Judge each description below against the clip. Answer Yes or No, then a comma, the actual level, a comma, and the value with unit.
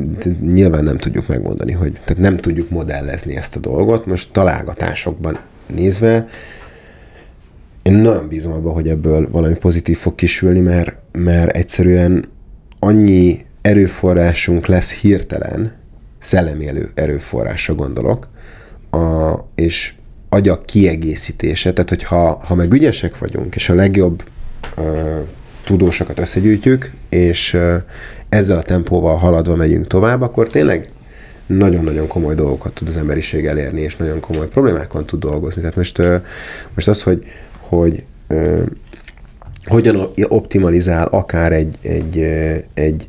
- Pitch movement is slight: No, average, 3.2 semitones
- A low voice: Yes, very low, 85 Hz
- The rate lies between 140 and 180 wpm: No, average, 120 wpm